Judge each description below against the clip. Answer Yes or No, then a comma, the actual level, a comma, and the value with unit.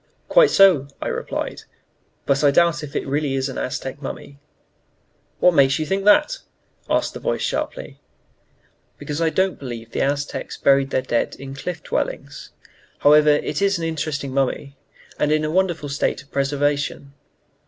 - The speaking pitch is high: No, medium, 145 Hz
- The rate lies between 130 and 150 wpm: No, average, 165 wpm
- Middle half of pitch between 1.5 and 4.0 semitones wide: Yes, average, 3.1 semitones